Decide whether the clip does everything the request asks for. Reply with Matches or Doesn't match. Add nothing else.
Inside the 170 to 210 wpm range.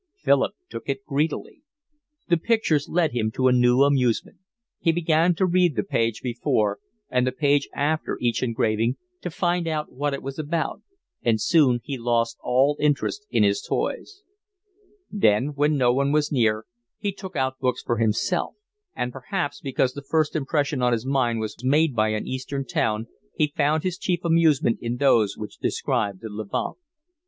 Matches